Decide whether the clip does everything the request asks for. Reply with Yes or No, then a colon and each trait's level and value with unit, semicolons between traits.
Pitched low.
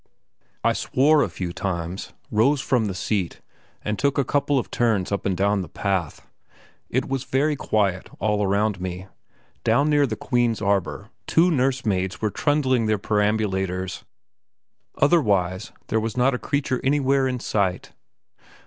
Yes: low, 110 Hz